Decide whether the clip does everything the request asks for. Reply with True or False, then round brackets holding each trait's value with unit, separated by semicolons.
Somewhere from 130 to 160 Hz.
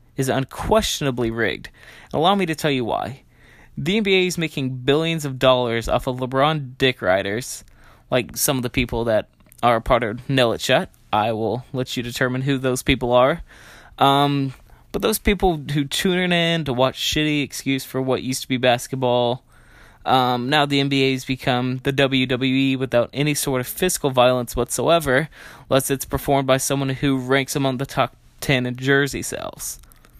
True (135 Hz)